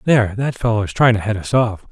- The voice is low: Yes, low, 110 Hz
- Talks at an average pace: No, fast, 285 wpm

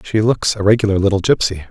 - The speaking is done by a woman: No, male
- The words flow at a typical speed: No, fast, 210 wpm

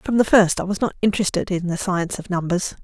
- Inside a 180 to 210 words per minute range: No, fast, 255 wpm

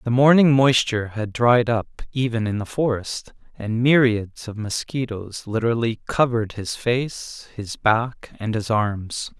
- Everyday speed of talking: Yes, average, 145 wpm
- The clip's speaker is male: Yes, male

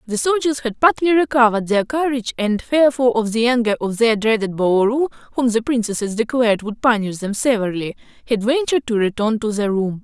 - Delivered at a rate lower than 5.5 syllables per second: No, 5.9 syllables/s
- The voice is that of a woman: Yes, female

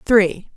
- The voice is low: No, high, 200 Hz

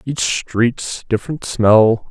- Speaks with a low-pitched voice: Yes, low, 115 Hz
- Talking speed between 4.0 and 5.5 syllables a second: No, 3.1 syllables/s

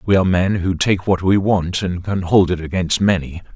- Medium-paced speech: No, fast, 235 wpm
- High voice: No, very low, 90 Hz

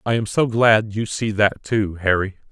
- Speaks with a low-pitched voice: Yes, low, 105 Hz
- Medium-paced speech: No, fast, 215 wpm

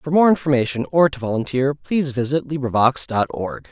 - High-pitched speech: No, low, 135 Hz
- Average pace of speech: Yes, average, 180 wpm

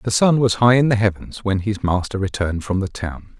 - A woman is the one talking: No, male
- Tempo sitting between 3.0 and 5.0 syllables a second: No, 5.7 syllables/s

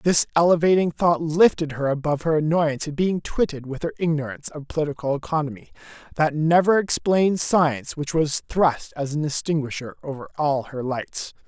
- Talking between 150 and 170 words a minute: Yes, average, 160 wpm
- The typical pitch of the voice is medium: Yes, medium, 155 Hz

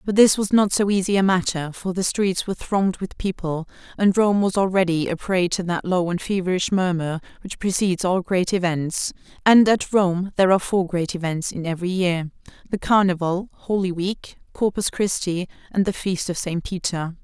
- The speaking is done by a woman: Yes, female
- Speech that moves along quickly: No, average, 190 wpm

